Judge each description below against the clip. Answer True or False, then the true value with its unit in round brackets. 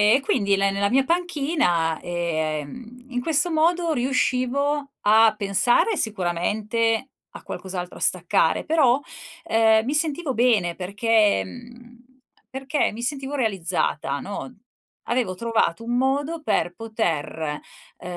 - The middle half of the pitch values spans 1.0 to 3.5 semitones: False (5.7 semitones)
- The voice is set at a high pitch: True (230 Hz)